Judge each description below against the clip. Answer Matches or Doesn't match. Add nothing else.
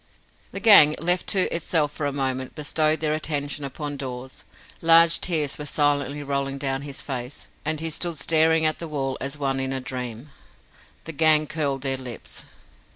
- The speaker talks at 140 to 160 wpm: Doesn't match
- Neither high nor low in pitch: Matches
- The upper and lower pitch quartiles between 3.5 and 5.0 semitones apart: Doesn't match